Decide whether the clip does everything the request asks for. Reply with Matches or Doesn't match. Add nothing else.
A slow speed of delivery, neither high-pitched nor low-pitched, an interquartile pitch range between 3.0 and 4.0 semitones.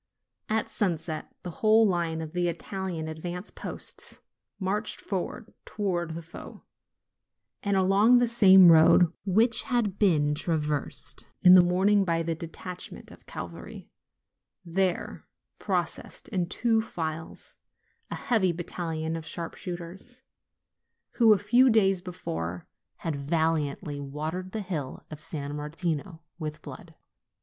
Matches